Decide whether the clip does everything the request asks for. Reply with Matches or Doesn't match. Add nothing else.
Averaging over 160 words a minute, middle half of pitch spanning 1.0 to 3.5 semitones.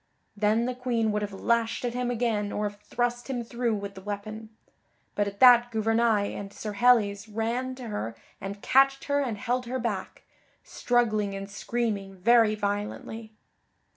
Matches